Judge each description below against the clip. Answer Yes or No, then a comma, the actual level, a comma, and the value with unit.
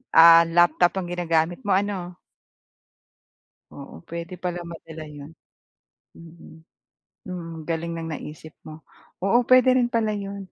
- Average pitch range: Yes, average, 3.0 semitones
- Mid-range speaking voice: Yes, medium, 170 Hz